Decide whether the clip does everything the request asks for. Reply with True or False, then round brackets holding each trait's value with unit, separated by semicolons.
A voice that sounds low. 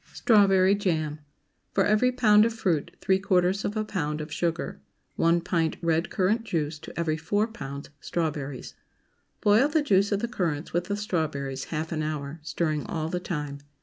False (170 Hz)